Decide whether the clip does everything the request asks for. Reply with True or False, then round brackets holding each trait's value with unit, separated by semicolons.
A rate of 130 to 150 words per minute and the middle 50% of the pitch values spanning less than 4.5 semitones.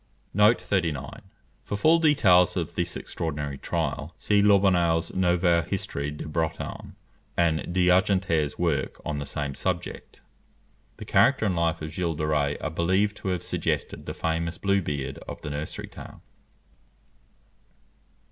True (135 wpm; 3.5 semitones)